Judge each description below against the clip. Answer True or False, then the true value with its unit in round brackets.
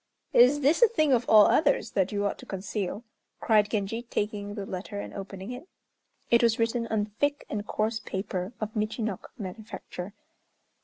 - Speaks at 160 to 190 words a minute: True (170 wpm)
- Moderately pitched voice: False (215 Hz)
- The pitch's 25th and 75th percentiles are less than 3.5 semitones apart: True (2.7 semitones)